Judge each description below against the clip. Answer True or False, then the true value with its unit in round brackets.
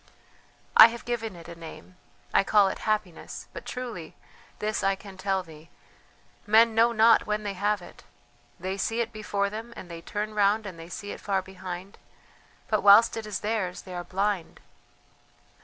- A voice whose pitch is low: False (200 Hz)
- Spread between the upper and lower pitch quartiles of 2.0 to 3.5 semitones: True (2.7 semitones)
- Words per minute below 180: False (185 wpm)